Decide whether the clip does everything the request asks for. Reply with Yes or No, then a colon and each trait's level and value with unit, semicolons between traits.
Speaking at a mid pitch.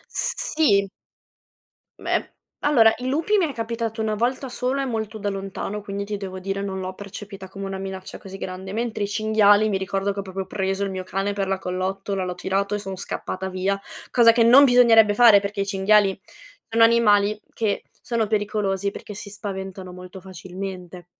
No: high, 200 Hz